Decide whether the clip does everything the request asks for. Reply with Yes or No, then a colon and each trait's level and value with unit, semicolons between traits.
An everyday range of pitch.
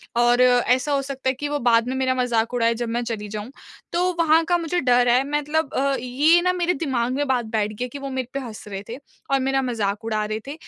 Yes: average, 3.3 semitones